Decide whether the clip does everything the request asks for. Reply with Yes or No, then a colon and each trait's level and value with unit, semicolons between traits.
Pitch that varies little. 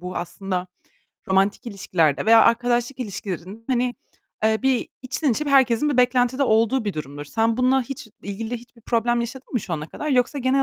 No: average, 4.3 semitones